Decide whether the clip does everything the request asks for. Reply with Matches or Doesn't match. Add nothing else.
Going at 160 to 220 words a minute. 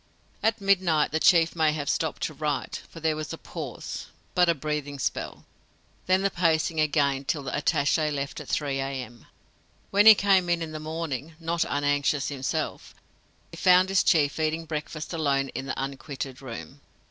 Matches